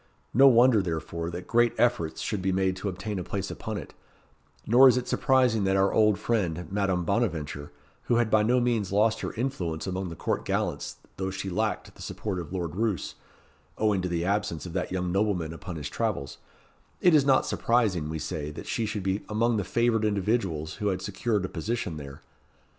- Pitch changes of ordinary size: Yes, average, 4.2 semitones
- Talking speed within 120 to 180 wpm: No, average, 200 wpm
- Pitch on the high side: No, low, 100 Hz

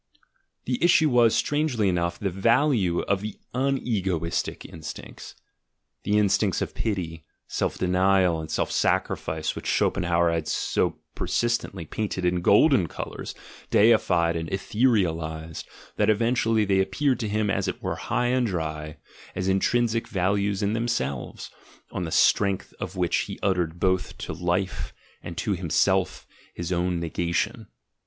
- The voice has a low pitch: Yes, very low, 95 Hz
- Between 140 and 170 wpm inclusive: Yes, average, 145 wpm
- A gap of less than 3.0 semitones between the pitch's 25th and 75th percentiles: No, average, 4.5 semitones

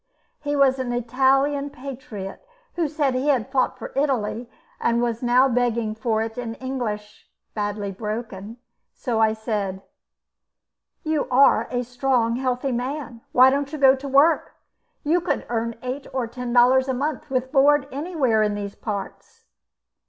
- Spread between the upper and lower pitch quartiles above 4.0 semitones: No, average, 3.2 semitones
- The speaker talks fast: No, average, 155 wpm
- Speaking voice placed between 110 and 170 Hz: No, very high, 250 Hz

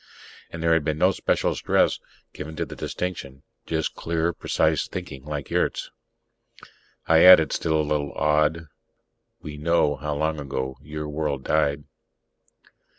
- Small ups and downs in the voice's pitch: Yes, narrow, 1.8 semitones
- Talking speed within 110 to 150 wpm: Yes, average, 140 wpm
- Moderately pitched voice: No, very low, 75 Hz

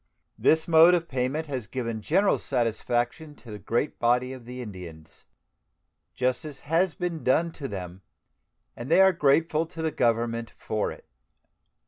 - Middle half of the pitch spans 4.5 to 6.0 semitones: Yes, wide, 5.5 semitones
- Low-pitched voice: Yes, low, 130 Hz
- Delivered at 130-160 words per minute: Yes, average, 150 wpm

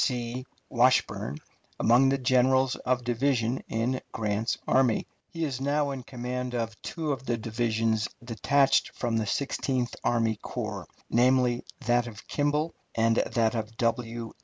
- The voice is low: Yes, low, 120 Hz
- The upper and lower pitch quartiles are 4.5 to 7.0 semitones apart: No, narrow, 2.5 semitones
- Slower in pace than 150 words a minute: Yes, average, 140 wpm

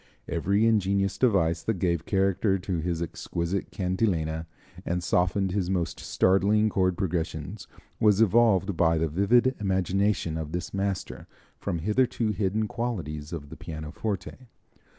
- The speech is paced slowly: Yes, slow, 130 wpm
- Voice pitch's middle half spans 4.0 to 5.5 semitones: No, average, 3.5 semitones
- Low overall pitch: Yes, very low, 95 Hz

